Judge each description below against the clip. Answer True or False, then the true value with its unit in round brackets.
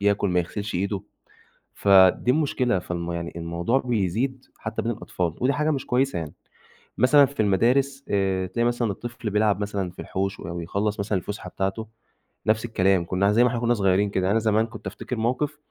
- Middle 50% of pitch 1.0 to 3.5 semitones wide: False (4.3 semitones)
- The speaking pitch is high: False (105 Hz)